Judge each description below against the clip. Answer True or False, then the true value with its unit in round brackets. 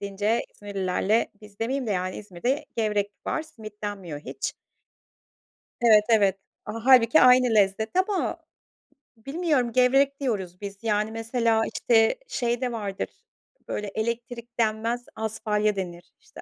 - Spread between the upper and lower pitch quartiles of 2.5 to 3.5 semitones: True (2.9 semitones)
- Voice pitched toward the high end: True (220 Hz)